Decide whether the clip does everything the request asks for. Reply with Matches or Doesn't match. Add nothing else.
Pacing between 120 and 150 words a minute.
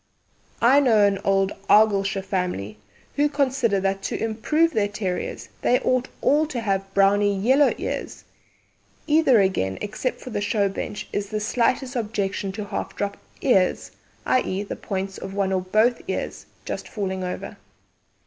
Doesn't match